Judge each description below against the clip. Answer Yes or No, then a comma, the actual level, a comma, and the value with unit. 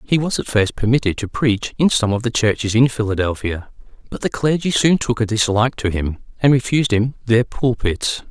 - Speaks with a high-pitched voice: No, low, 115 Hz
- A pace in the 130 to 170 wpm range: No, average, 200 wpm